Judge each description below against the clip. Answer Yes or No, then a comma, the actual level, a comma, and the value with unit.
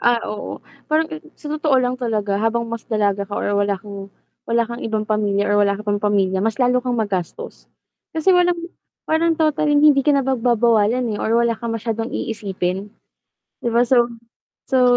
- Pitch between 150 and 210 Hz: No, high, 230 Hz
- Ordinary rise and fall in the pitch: Yes, average, 3.6 semitones